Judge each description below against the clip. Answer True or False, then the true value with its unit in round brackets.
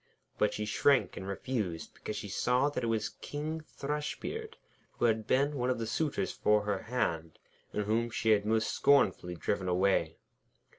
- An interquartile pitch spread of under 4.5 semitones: False (4.8 semitones)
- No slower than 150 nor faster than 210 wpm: True (170 wpm)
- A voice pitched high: False (110 Hz)